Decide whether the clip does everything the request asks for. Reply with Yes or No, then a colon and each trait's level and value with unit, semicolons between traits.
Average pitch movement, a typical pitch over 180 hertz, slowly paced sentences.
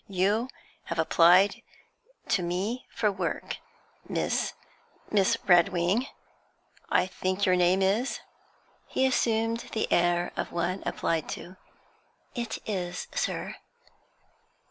Yes: average, 3.8 semitones; high, 190 Hz; slow, 105 wpm